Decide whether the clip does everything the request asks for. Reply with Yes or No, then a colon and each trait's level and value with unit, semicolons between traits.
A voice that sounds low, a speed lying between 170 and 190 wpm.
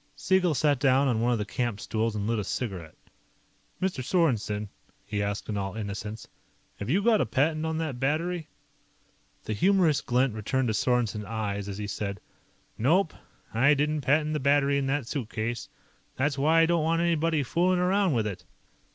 Yes: low, 130 Hz; average, 180 wpm